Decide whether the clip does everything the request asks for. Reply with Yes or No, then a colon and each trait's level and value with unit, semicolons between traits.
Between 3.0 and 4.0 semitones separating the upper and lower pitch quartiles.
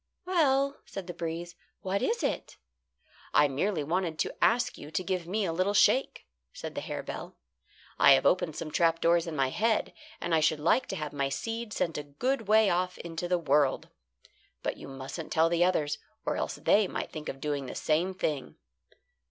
No: average, 4.7 semitones